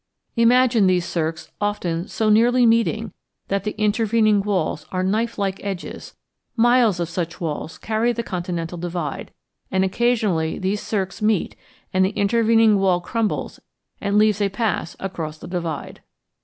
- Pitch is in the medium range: No, high, 200 Hz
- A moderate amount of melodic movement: Yes, average, 4.0 semitones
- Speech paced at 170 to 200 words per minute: No, average, 145 wpm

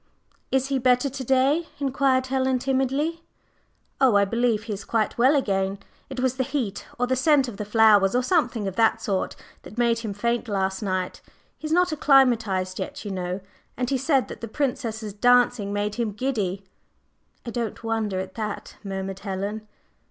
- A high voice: Yes, high, 235 Hz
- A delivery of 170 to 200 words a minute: Yes, average, 180 wpm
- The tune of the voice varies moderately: Yes, average, 4.4 semitones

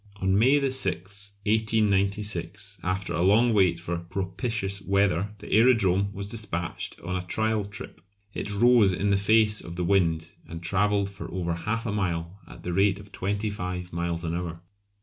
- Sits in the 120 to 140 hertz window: No, low, 100 Hz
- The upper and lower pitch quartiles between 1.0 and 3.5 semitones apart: Yes, average, 2.7 semitones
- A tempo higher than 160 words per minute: Yes, average, 170 wpm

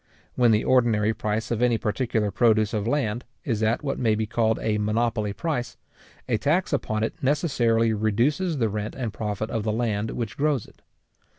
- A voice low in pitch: Yes, low, 115 Hz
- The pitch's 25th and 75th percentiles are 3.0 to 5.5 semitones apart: No, narrow, 2.4 semitones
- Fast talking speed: No, average, 185 wpm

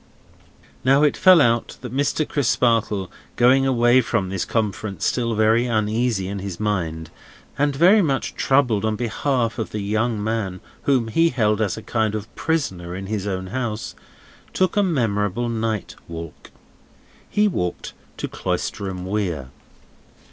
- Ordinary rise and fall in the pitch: Yes, average, 4.3 semitones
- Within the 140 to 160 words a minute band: Yes, average, 150 wpm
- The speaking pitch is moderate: No, low, 110 Hz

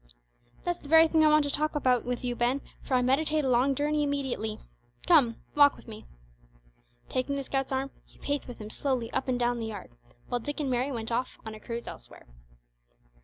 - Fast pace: Yes, fast, 215 wpm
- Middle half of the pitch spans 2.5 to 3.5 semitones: Yes, average, 3.2 semitones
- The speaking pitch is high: Yes, very high, 265 Hz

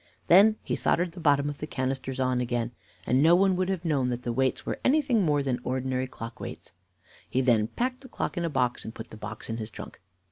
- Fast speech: Yes, fast, 240 wpm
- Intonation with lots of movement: Yes, wide, 5.8 semitones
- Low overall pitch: Yes, low, 130 Hz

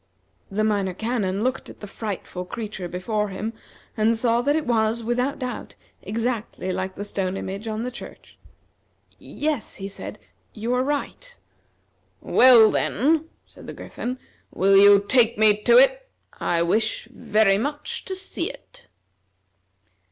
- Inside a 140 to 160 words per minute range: Yes, average, 145 wpm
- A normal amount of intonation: Yes, average, 4.1 semitones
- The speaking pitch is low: No, high, 220 Hz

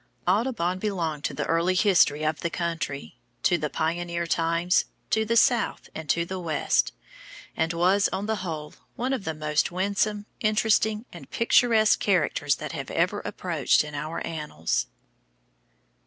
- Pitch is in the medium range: Yes, medium, 175 Hz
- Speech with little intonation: No, average, 4.6 semitones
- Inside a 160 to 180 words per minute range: No, average, 150 wpm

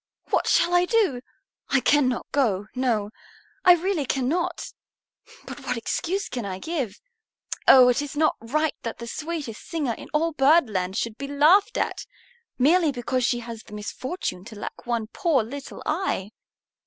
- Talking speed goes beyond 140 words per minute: Yes, average, 160 wpm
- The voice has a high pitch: Yes, very high, 270 Hz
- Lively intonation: Yes, wide, 5.7 semitones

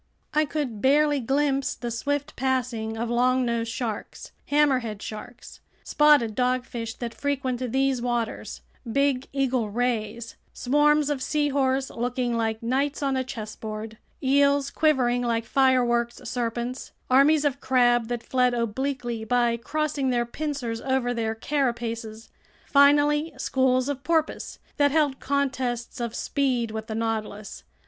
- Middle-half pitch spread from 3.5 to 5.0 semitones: No, average, 3.1 semitones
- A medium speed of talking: No, slow, 130 wpm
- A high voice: Yes, very high, 255 Hz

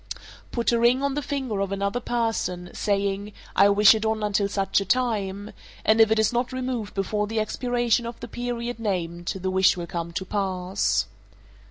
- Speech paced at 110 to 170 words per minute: No, average, 190 wpm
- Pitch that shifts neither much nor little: Yes, average, 3.3 semitones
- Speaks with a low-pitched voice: No, high, 210 Hz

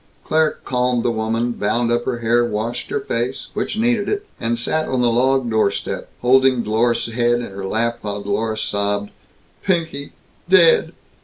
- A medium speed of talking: Yes, average, 165 wpm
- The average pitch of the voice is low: Yes, low, 120 Hz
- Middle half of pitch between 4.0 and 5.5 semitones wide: No, average, 2.9 semitones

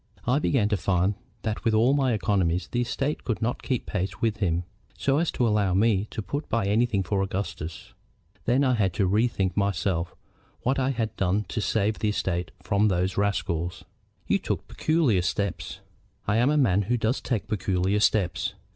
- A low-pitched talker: Yes, low, 105 Hz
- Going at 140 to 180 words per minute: No, average, 190 wpm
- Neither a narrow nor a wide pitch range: Yes, average, 4.0 semitones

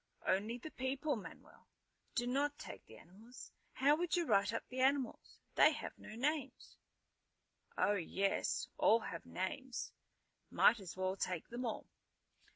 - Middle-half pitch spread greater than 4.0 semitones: Yes, wide, 5.5 semitones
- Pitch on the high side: Yes, high, 240 Hz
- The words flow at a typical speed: Yes, average, 150 wpm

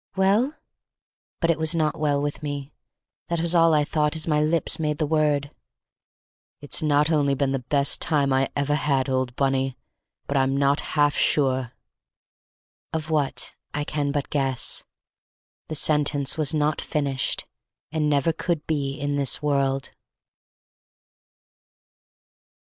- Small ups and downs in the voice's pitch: Yes, narrow, 1.9 semitones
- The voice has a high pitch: No, medium, 145 Hz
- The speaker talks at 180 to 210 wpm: No, average, 145 wpm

